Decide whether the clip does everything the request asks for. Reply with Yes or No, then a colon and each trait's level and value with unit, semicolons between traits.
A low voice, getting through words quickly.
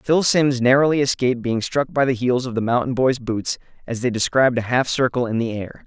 Yes: low, 125 Hz; fast, 235 wpm